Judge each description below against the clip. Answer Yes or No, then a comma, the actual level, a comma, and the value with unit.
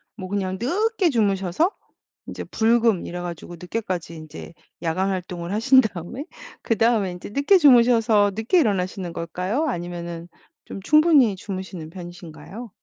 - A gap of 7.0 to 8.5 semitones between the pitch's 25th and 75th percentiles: No, average, 5.2 semitones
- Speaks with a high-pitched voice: Yes, high, 195 Hz